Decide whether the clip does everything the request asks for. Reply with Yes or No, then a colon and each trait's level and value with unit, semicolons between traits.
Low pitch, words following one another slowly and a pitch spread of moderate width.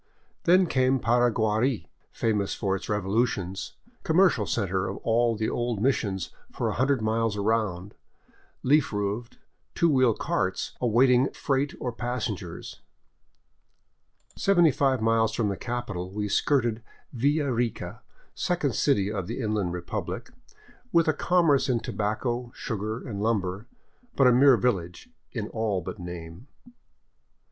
Yes: low, 115 Hz; slow, 130 wpm; average, 4.2 semitones